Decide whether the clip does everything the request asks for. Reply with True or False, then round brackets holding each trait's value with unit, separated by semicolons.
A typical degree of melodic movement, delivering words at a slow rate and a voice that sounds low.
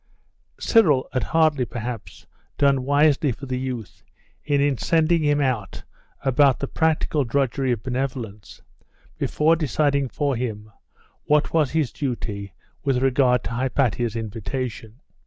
True (3.3 semitones; 125 wpm; 130 Hz)